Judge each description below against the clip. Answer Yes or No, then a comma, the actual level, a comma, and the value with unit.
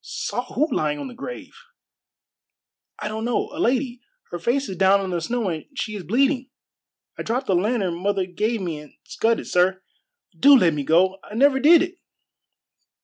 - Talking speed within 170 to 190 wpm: Yes, average, 185 wpm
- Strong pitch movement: Yes, wide, 5.8 semitones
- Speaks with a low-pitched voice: No, high, 215 Hz